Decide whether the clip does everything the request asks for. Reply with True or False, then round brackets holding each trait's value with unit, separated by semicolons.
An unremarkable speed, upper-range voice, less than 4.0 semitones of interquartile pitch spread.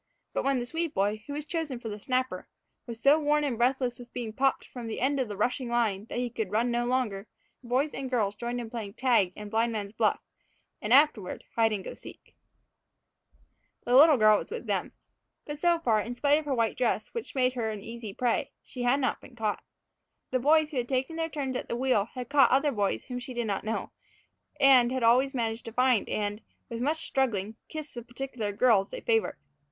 False (220 wpm; 245 Hz; 3.4 semitones)